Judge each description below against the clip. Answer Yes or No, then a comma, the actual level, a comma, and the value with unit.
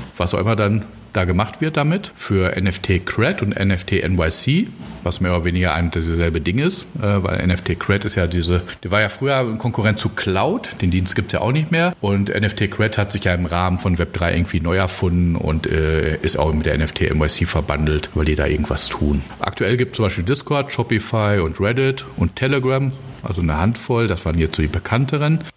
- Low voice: Yes, very low, 95 Hz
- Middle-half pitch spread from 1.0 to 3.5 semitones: No, average, 4.7 semitones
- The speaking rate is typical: No, fast, 215 wpm